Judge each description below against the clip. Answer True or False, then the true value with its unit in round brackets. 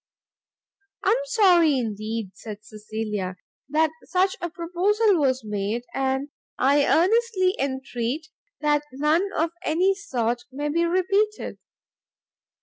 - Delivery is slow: True (115 wpm)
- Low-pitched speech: False (300 Hz)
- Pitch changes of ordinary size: False (7.5 semitones)